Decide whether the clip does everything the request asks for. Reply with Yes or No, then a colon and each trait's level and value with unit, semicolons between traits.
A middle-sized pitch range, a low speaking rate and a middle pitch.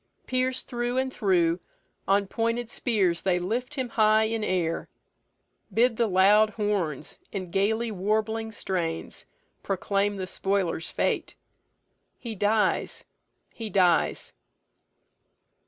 No: average, 3.4 semitones; slow, 110 wpm; high, 210 Hz